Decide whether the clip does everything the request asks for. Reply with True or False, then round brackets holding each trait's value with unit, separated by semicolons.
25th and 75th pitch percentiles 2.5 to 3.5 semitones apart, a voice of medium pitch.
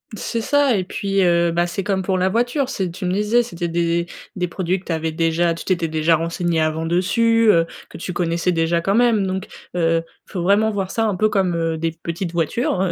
True (3.0 semitones; 180 Hz)